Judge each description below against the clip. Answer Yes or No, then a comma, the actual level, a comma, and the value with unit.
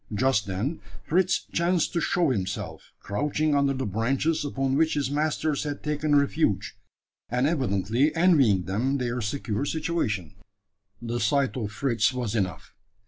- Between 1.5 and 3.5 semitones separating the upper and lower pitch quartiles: No, average, 5.3 semitones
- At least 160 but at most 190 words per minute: No, average, 140 wpm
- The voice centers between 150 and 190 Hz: No, low, 135 Hz